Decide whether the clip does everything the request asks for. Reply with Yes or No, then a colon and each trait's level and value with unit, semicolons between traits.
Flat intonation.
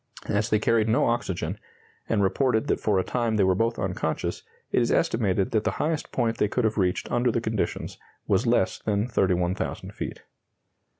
No: average, 3.3 semitones